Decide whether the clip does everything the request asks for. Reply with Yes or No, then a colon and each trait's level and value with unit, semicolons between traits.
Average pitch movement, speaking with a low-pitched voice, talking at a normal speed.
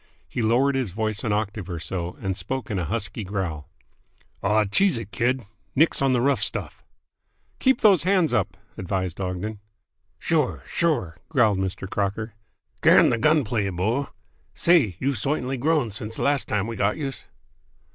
No: wide, 5.8 semitones; low, 110 Hz; average, 165 wpm